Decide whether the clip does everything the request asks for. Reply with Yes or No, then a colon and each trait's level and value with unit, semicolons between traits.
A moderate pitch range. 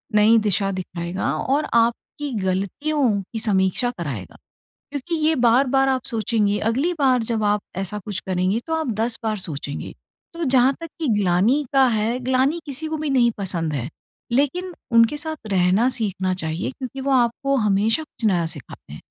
No: wide, 5.9 semitones